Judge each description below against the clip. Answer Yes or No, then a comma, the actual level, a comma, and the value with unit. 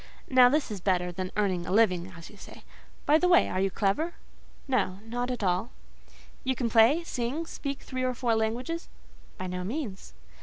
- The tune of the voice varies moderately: No, wide, 5.7 semitones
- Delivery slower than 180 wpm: No, average, 185 wpm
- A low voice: No, high, 225 Hz